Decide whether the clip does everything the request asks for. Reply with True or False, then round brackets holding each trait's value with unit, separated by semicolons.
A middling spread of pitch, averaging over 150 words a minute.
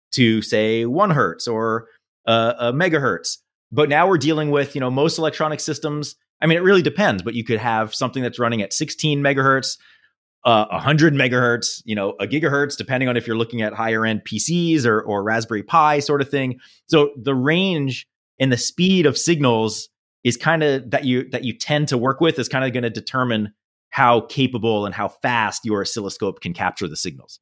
True (4.7 semitones; 200 wpm)